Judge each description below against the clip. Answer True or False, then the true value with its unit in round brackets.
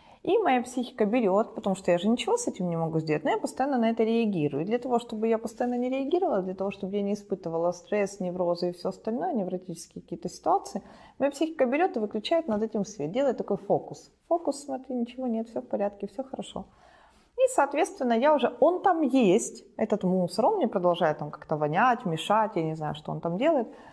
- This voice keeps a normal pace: False (215 wpm)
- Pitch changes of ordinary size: False (6.3 semitones)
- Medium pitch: False (225 Hz)